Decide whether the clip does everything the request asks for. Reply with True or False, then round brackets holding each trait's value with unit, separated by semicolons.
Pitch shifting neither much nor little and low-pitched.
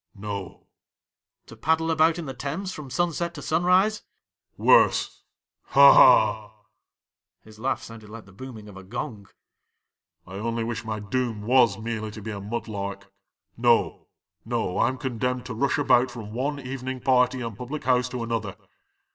True (3.9 semitones; 120 Hz)